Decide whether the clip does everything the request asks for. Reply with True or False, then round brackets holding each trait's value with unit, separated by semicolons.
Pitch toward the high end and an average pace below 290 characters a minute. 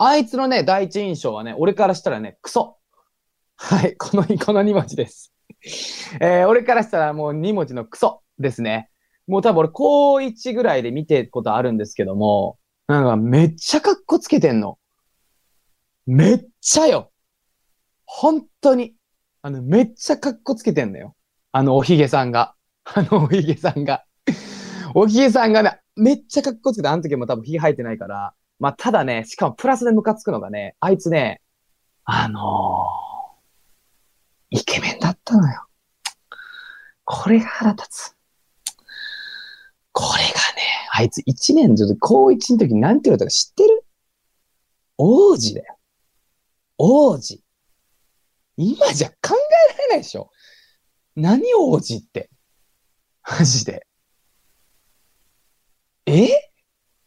True (205 Hz; 270 characters per minute)